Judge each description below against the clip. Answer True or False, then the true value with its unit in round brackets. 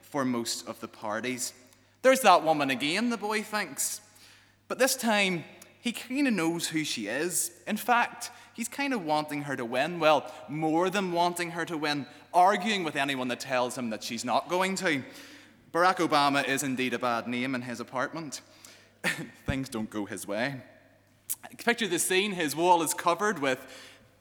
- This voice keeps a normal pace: True (180 wpm)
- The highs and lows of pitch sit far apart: True (7.0 semitones)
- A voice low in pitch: False (155 Hz)